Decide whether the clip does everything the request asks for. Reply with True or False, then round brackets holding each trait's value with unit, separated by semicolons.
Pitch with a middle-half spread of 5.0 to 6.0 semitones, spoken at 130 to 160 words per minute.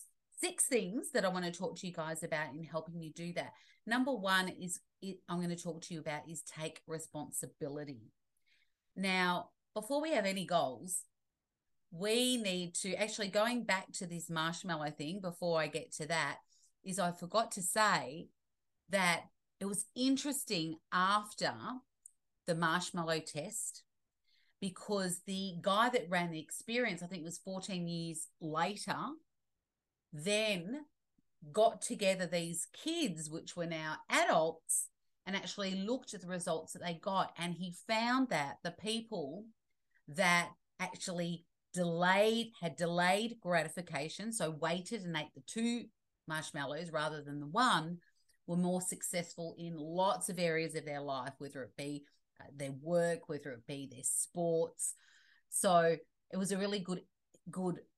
False (3.8 semitones; 150 wpm)